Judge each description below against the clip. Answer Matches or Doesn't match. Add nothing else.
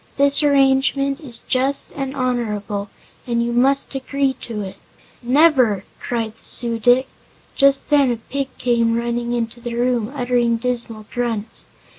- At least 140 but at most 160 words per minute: Matches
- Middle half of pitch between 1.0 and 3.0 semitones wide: Matches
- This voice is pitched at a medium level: Doesn't match